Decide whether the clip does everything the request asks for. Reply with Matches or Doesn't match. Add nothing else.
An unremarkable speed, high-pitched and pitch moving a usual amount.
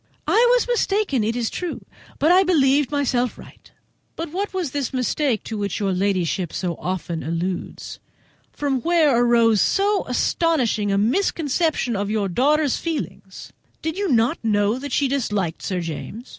Doesn't match